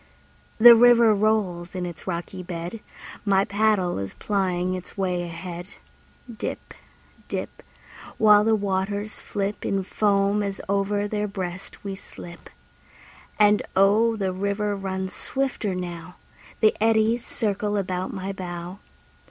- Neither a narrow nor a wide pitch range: No, narrow, 2.3 semitones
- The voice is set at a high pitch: Yes, high, 195 Hz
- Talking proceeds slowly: Yes, slow, 125 wpm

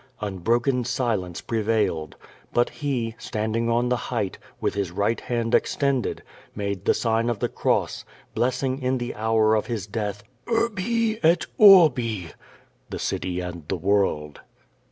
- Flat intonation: No, average, 3.9 semitones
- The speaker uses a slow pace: No, average, 145 wpm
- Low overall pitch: Yes, low, 115 Hz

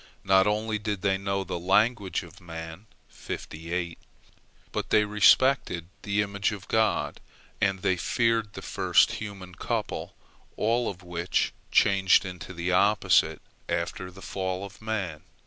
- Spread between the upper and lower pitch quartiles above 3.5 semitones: No, narrow, 2.5 semitones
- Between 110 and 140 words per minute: Yes, slow, 135 wpm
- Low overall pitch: Yes, very low, 95 Hz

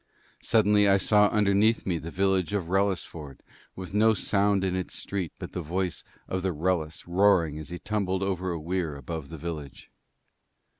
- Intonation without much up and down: No, average, 3.1 semitones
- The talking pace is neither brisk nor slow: Yes, average, 170 wpm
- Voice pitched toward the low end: Yes, very low, 95 Hz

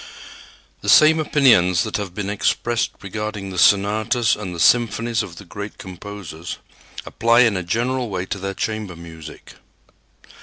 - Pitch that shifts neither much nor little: Yes, average, 4.0 semitones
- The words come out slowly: No, average, 150 wpm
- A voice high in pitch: No, low, 105 Hz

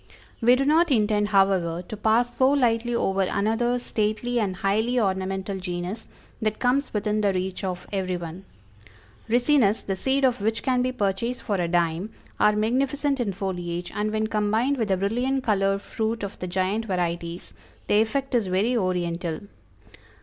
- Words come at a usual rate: Yes, average, 165 wpm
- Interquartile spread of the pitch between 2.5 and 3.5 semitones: No, average, 4.3 semitones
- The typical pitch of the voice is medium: No, high, 210 Hz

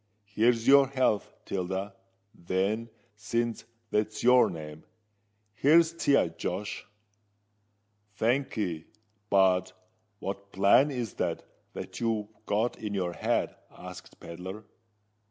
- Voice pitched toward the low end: Yes, low, 105 Hz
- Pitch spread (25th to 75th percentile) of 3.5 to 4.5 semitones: Yes, average, 3.9 semitones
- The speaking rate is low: Yes, slow, 100 wpm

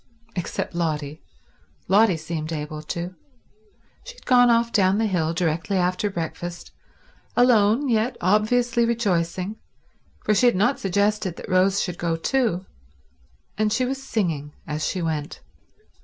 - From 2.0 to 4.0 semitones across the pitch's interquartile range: No, average, 5.1 semitones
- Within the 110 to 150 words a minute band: Yes, average, 140 wpm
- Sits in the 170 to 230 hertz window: Yes, high, 190 Hz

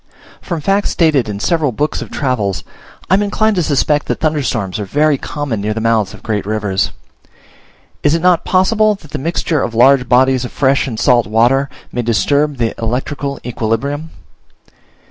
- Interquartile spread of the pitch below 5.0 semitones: No, average, 5.3 semitones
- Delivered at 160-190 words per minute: Yes, average, 175 wpm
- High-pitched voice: No, low, 135 Hz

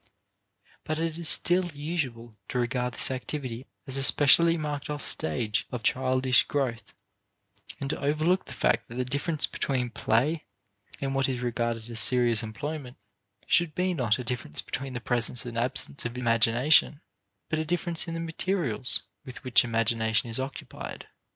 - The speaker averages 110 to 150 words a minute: No, average, 165 wpm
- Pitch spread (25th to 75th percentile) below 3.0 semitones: No, average, 4.3 semitones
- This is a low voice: Yes, low, 130 Hz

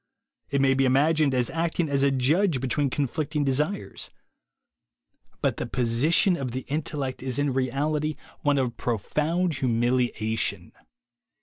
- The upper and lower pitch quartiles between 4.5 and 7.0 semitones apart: No, average, 3.1 semitones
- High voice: No, low, 135 Hz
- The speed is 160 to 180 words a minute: Yes, average, 165 wpm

